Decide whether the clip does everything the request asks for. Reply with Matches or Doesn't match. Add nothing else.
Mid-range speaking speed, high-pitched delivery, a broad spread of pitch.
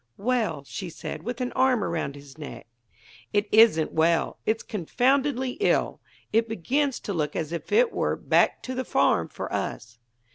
Matches